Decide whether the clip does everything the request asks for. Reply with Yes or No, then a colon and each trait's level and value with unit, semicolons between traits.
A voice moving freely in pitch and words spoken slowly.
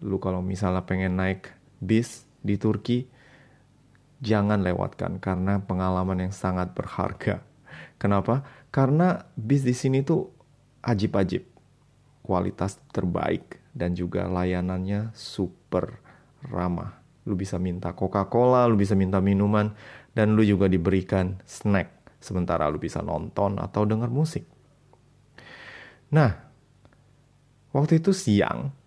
No: wide, 5.8 semitones; average, 110 wpm